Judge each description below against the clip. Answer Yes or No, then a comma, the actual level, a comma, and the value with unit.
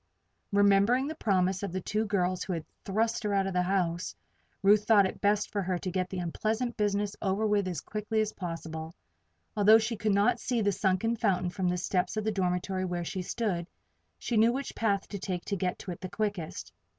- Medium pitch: No, high, 200 Hz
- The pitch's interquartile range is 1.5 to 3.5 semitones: Yes, average, 2.8 semitones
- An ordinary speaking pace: No, fast, 210 wpm